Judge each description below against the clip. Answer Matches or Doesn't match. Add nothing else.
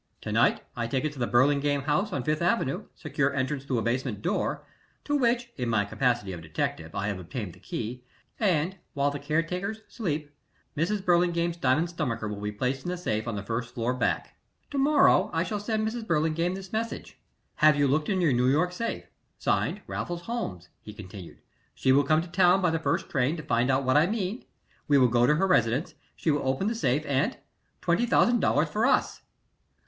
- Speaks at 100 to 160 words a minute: Doesn't match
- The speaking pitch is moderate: Matches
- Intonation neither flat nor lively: Doesn't match